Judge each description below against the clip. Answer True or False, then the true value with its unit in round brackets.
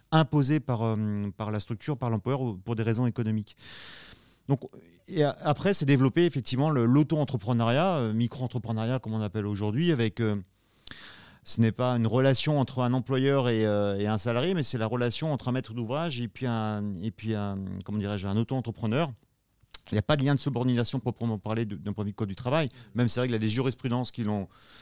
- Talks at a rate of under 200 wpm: False (215 wpm)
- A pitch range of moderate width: True (3.5 semitones)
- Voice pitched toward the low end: True (120 Hz)